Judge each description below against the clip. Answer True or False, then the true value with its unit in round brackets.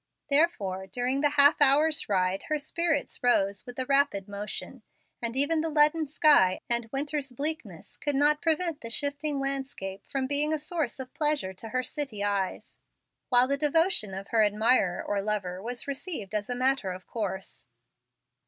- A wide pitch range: True (6.4 semitones)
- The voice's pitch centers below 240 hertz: False (265 Hz)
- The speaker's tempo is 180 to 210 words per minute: False (170 wpm)